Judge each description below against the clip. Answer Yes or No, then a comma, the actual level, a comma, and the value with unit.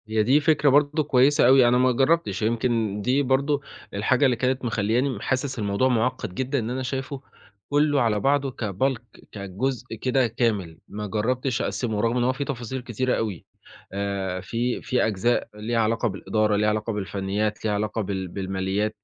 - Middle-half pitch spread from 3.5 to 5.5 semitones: Yes, average, 3.9 semitones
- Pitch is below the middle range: Yes, low, 115 Hz